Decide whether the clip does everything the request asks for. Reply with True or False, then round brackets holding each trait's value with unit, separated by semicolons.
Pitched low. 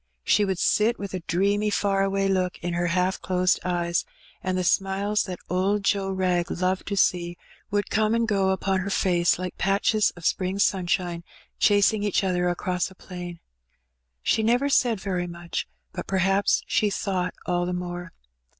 False (190 Hz)